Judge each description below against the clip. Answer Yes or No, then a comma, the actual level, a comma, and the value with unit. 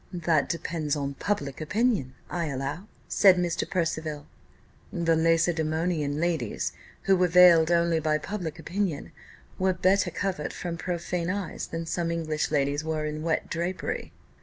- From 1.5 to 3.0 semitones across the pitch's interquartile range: Yes, narrow, 2.6 semitones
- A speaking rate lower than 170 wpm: Yes, average, 140 wpm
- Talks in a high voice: No, medium, 165 Hz